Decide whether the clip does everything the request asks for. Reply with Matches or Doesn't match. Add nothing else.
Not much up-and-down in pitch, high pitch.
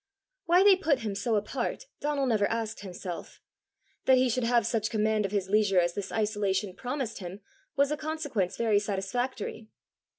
Doesn't match